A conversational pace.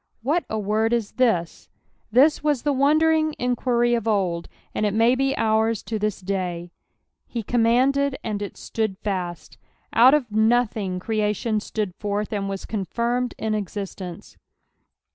Yes: average, 150 wpm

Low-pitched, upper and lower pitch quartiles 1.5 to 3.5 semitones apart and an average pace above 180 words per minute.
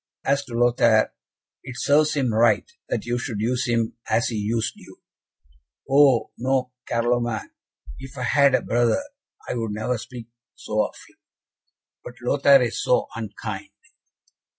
No: low, 120 Hz; narrow, 2.6 semitones; average, 150 wpm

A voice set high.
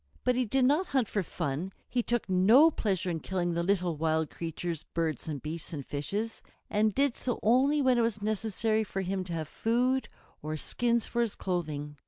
Yes: high, 195 Hz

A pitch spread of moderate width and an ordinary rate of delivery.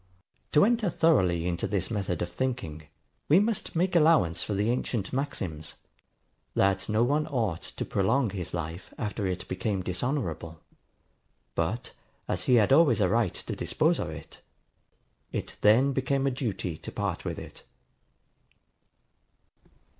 No: wide, 7.3 semitones; average, 145 wpm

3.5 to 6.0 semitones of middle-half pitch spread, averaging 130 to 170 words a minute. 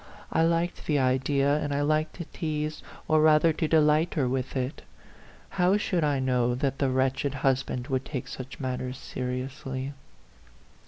No: average, 2.9 semitones; average, 160 wpm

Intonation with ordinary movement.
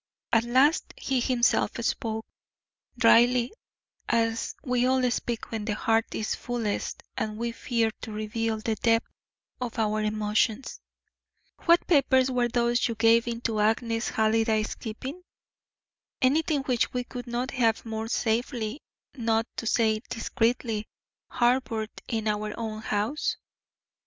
No: narrow, 2.0 semitones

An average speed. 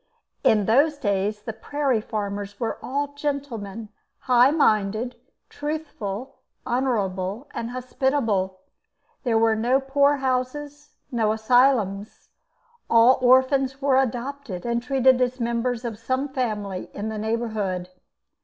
No: slow, 115 wpm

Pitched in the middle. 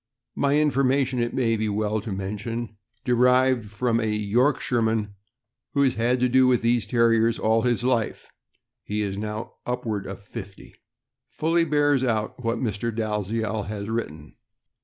No: low, 115 Hz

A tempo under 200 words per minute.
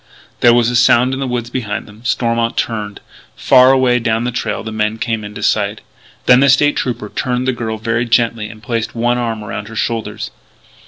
No: fast, 205 wpm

